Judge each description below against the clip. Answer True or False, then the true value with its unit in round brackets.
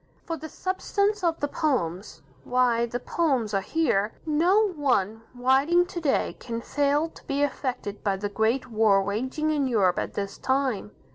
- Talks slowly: False (165 wpm)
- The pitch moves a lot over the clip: True (6.4 semitones)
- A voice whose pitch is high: True (260 Hz)